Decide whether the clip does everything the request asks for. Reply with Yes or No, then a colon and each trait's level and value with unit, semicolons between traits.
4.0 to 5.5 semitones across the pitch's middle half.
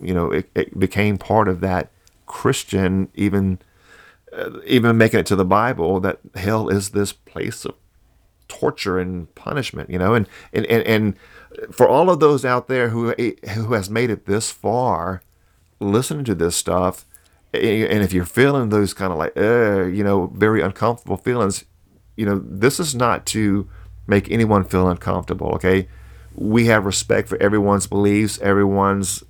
No: average, 2.9 semitones